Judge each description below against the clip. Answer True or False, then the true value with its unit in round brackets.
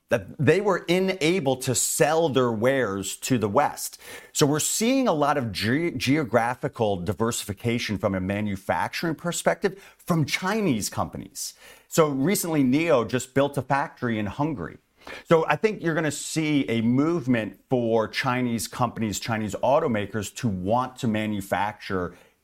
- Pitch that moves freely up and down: True (5.8 semitones)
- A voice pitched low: True (130 Hz)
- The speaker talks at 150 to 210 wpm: False (140 wpm)